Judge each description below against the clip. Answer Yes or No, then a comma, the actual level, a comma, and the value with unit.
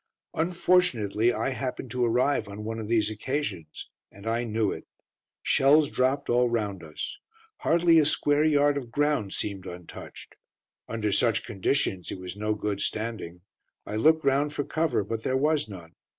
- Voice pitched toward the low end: Yes, low, 115 Hz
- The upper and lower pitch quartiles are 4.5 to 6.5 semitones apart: Yes, wide, 5.5 semitones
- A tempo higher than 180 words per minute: No, average, 165 wpm